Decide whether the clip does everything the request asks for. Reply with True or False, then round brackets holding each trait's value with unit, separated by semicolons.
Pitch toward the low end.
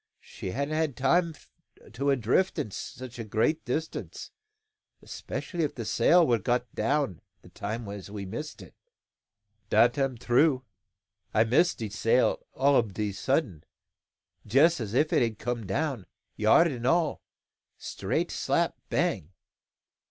True (125 Hz)